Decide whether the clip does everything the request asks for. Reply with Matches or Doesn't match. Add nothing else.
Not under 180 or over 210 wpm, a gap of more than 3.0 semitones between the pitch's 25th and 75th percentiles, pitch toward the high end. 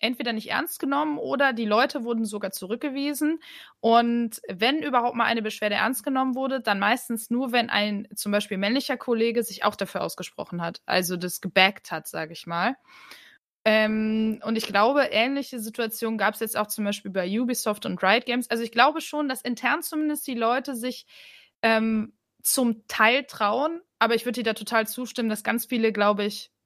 Matches